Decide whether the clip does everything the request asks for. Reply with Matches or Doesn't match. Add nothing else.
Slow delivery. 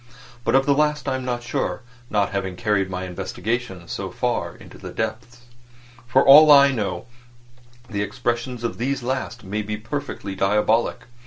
Doesn't match